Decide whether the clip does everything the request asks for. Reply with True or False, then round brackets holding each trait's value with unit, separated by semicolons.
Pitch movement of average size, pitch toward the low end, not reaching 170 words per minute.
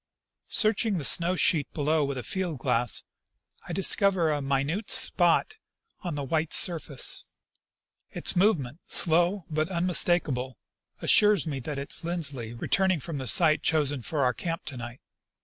False (4.3 semitones; 160 Hz; 150 wpm)